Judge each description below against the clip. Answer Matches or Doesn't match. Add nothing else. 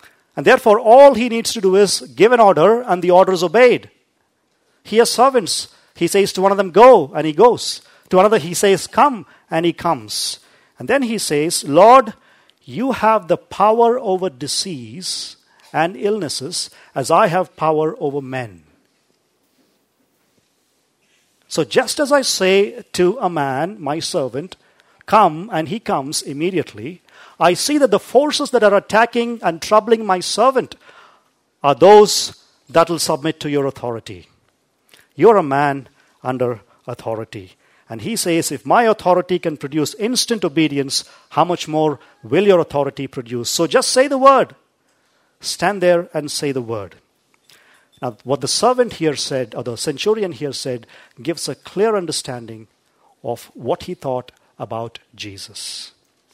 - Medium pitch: Matches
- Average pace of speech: Matches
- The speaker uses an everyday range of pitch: Doesn't match